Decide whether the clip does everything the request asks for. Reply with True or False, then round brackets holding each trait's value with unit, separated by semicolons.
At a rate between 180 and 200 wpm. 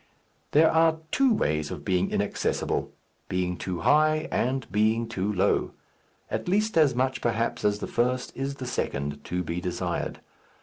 False (160 wpm)